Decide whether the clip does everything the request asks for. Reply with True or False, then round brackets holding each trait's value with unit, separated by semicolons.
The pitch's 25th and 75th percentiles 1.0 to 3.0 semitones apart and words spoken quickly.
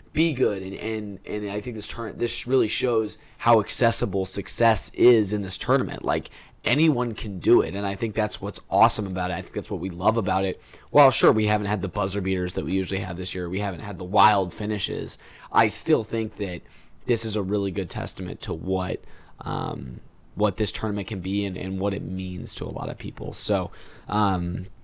True (2.7 semitones; 215 wpm)